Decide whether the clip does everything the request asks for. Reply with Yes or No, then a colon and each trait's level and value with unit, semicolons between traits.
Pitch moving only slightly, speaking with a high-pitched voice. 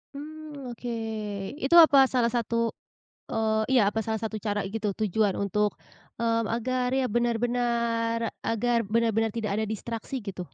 Yes: narrow, 1.8 semitones; high, 230 Hz